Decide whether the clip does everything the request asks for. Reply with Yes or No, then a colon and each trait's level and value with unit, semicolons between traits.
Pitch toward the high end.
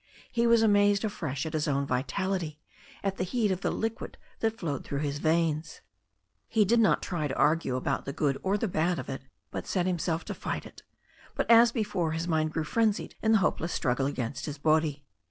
No: medium, 165 Hz